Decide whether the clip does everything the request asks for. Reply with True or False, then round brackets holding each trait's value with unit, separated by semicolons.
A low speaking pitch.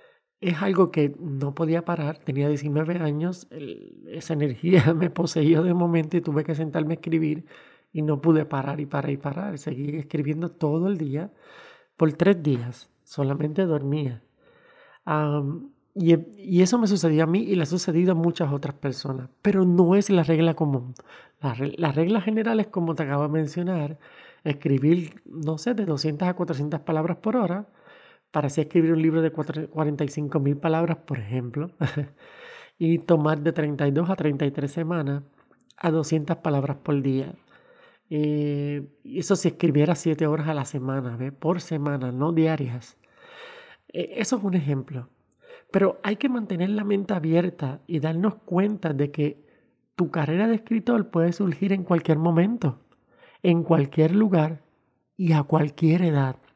False (160 Hz)